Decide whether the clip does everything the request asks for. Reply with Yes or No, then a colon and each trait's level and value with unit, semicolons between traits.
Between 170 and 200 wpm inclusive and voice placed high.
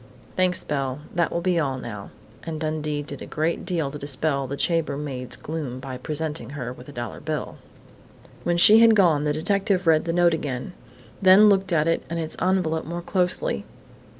No: average, 185 wpm; medium, 160 Hz